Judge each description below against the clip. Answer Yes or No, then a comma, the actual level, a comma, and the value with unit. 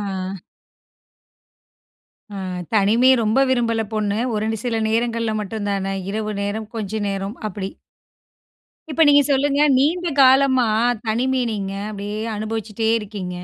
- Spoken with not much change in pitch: No, average, 3.6 semitones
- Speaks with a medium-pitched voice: No, high, 220 Hz